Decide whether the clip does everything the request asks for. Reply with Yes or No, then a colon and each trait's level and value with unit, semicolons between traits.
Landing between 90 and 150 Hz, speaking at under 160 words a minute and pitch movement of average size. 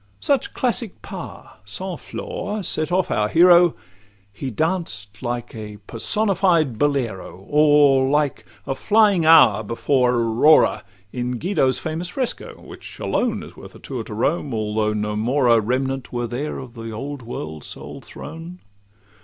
No: low, 135 Hz; average, 140 wpm; wide, 6.5 semitones